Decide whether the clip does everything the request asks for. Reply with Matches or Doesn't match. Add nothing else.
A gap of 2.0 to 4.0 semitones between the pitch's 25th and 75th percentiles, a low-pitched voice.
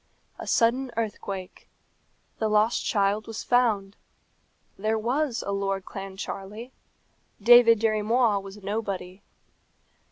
Doesn't match